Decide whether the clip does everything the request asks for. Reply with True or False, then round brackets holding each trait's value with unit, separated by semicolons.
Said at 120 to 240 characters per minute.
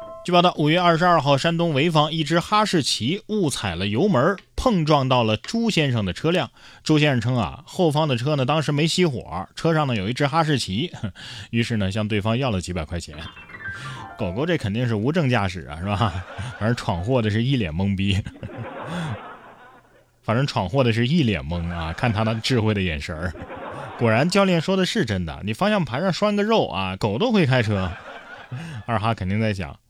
False (280 characters per minute)